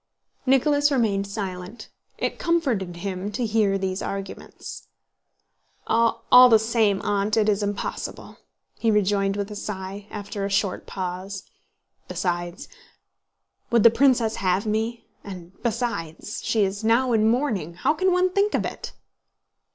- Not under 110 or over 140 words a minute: Yes, slow, 135 wpm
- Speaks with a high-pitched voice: Yes, high, 210 Hz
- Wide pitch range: No, average, 3.2 semitones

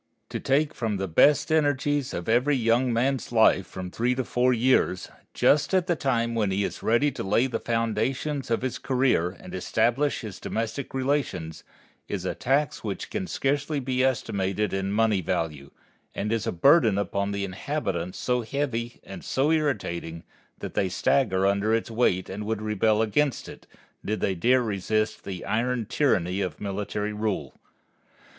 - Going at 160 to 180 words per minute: Yes, average, 170 wpm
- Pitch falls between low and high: No, low, 115 Hz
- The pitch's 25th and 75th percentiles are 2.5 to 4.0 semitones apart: No, average, 5.1 semitones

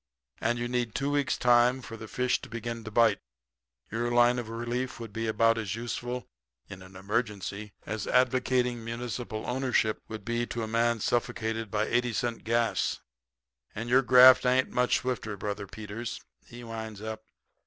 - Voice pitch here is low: Yes, low, 115 Hz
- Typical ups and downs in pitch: No, narrow, 1.9 semitones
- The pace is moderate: Yes, average, 165 wpm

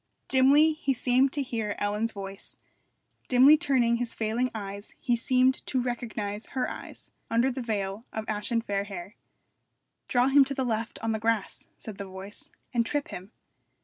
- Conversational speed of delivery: Yes, average, 170 wpm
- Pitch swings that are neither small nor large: Yes, average, 3.8 semitones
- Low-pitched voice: No, high, 230 Hz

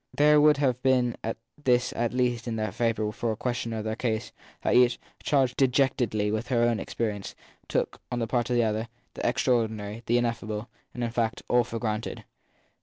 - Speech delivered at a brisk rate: No, average, 185 wpm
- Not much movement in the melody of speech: Yes, narrow, 2.0 semitones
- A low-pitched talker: Yes, low, 120 Hz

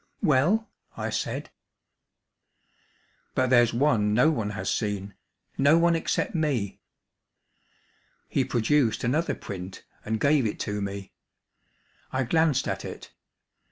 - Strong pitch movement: Yes, wide, 6.3 semitones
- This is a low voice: Yes, low, 125 Hz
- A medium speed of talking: No, slow, 120 wpm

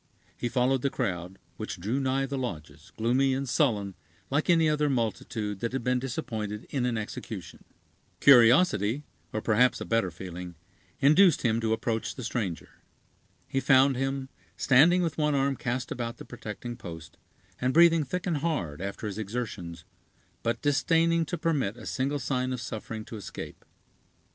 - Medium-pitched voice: No, low, 125 Hz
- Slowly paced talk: No, average, 165 wpm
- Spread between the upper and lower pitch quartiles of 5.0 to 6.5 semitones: No, average, 4.4 semitones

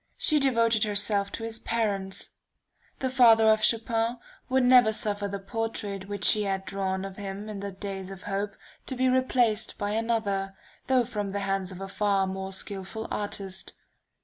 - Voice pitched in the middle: No, high, 205 Hz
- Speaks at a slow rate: No, average, 175 wpm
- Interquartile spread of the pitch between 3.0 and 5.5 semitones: No, narrow, 2.6 semitones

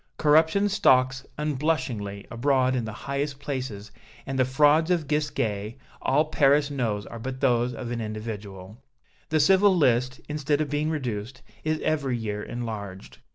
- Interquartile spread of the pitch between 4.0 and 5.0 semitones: Yes, average, 4.7 semitones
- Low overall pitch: Yes, low, 130 Hz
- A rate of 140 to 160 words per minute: Yes, average, 150 wpm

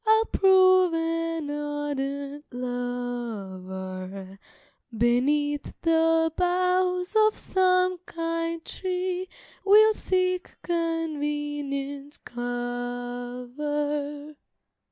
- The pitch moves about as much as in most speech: No, wide, 6.5 semitones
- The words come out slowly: Yes, slow, 65 wpm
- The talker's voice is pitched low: No, very high, 295 Hz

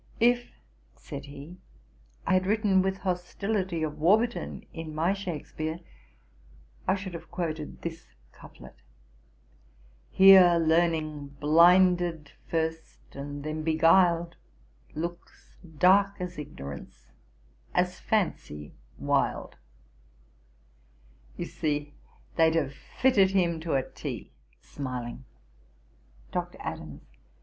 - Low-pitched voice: No, medium, 165 Hz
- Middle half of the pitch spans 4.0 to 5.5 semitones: No, average, 3.6 semitones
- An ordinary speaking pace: No, slow, 100 wpm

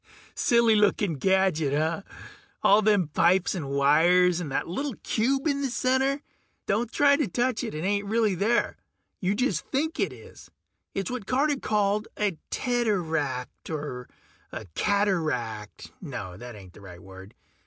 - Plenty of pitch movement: Yes, wide, 7.8 semitones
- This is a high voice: Yes, high, 195 Hz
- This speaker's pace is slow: No, average, 155 wpm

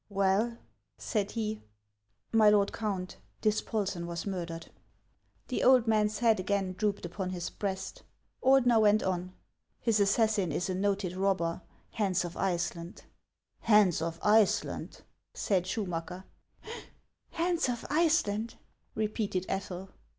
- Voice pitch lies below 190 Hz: No, high, 200 Hz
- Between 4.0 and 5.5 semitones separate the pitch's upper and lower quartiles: No, average, 3.1 semitones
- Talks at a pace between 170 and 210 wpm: No, average, 145 wpm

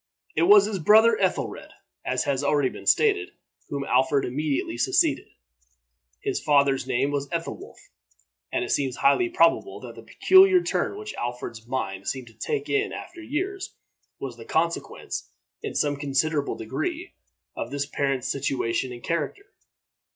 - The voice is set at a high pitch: No, medium, 145 Hz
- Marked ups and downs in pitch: Yes, wide, 8.3 semitones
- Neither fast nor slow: Yes, average, 150 wpm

